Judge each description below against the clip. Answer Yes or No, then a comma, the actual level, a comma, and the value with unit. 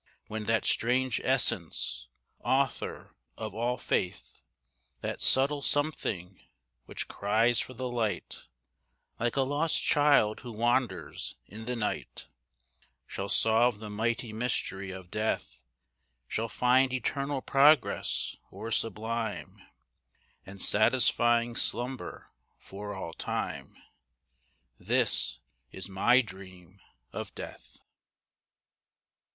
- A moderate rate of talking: No, slow, 100 wpm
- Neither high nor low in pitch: No, low, 115 Hz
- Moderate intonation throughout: Yes, average, 3.6 semitones